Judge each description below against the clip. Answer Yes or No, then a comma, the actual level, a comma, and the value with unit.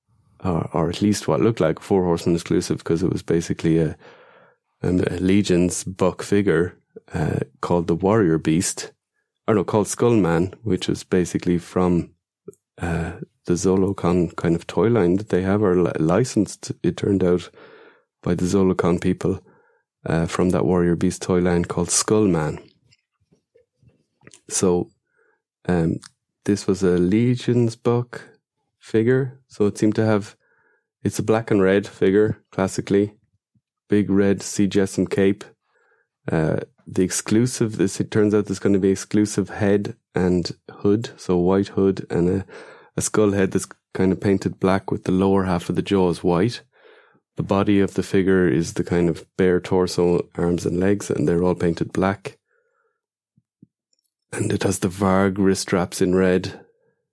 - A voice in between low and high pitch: No, very low, 95 Hz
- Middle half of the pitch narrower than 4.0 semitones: Yes, average, 2.9 semitones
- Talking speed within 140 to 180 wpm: Yes, average, 160 wpm